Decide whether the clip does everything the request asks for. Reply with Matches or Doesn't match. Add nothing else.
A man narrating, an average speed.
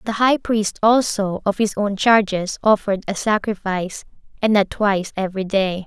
Doesn't match